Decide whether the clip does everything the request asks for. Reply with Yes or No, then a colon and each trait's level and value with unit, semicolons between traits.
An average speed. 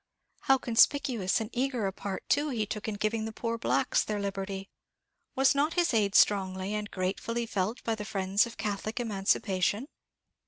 Yes: average, 170 wpm